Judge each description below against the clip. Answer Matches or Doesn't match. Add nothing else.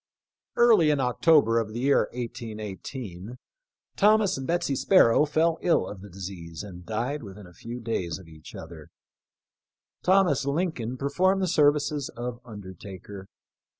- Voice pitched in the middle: Doesn't match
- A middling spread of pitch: Doesn't match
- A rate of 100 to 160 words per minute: Matches